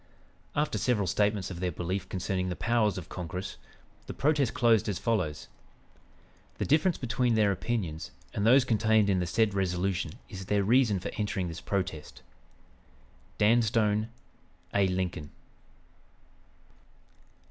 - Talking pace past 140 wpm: No, slow, 135 wpm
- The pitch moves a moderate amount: Yes, average, 3.8 semitones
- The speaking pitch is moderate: No, low, 100 Hz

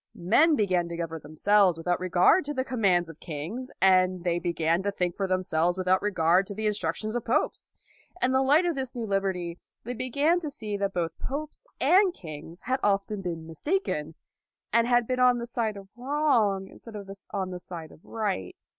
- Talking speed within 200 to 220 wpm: Yes, fast, 205 wpm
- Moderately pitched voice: No, high, 195 Hz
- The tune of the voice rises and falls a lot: Yes, wide, 6.0 semitones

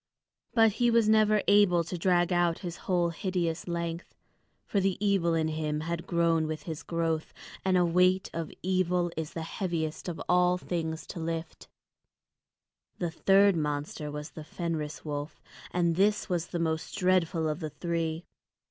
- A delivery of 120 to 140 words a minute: No, average, 165 wpm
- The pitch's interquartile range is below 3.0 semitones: Yes, narrow, 2.4 semitones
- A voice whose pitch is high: No, medium, 170 Hz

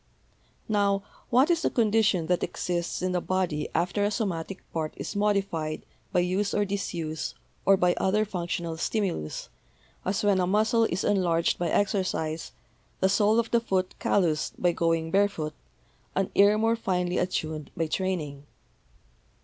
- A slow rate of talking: No, average, 155 wpm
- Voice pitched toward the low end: No, medium, 185 Hz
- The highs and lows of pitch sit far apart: No, average, 3.5 semitones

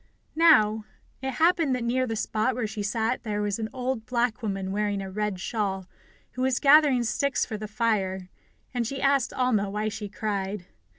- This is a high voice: Yes, high, 220 Hz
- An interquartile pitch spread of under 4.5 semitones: Yes, average, 3.6 semitones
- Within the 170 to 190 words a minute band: Yes, average, 185 wpm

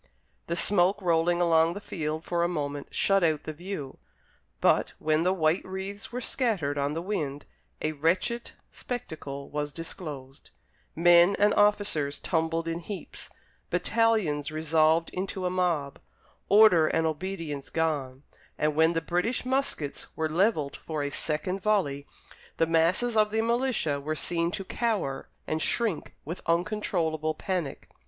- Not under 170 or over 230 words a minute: No, average, 145 wpm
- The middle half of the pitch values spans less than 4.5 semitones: Yes, average, 4.1 semitones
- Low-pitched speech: No, medium, 165 Hz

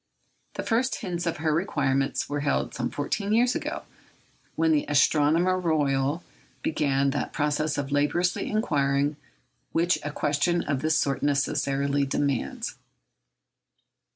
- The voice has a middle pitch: Yes, medium, 150 Hz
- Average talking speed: No, slow, 125 wpm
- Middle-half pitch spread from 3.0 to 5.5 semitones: Yes, average, 3.3 semitones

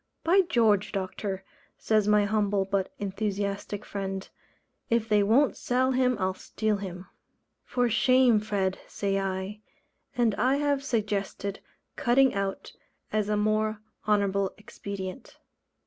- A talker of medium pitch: No, high, 210 Hz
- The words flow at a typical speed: No, slow, 125 wpm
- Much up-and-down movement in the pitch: No, average, 2.9 semitones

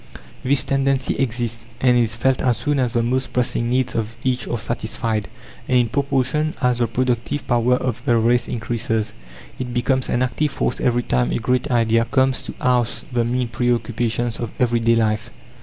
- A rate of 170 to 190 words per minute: Yes, average, 180 wpm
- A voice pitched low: Yes, low, 120 Hz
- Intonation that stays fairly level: Yes, narrow, 1.8 semitones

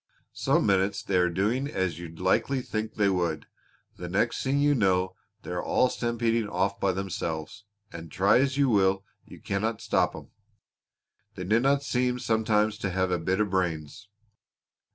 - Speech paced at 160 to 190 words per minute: Yes, average, 170 wpm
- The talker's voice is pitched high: No, low, 100 Hz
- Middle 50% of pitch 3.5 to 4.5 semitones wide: Yes, average, 4.0 semitones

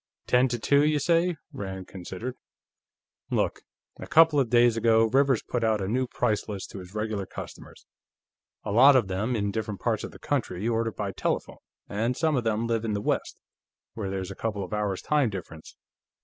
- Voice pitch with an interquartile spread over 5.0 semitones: No, average, 4.0 semitones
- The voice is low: Yes, low, 110 Hz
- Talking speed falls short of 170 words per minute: No, average, 195 wpm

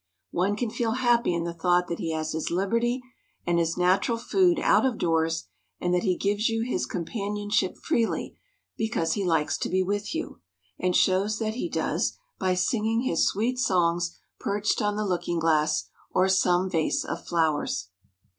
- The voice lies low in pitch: No, high, 190 Hz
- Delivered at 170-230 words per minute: Yes, average, 175 wpm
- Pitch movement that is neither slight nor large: Yes, average, 4.5 semitones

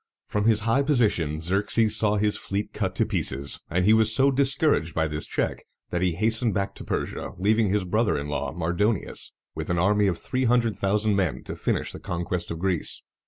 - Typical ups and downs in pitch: Yes, average, 4.1 semitones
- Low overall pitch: Yes, low, 100 Hz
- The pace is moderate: No, fast, 215 wpm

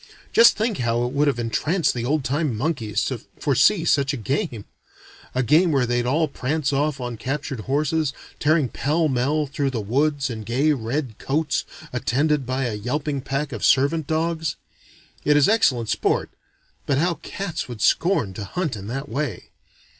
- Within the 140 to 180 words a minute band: Yes, average, 170 wpm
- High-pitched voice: No, medium, 140 Hz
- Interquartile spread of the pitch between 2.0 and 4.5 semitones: Yes, average, 4.1 semitones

